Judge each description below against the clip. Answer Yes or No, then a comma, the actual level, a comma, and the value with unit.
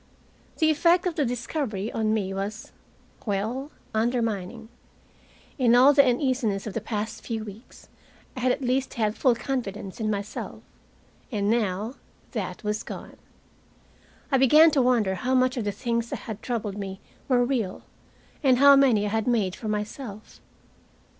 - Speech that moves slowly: No, average, 160 wpm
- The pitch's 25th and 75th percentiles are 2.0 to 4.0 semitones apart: Yes, average, 3.6 semitones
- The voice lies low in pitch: No, high, 230 Hz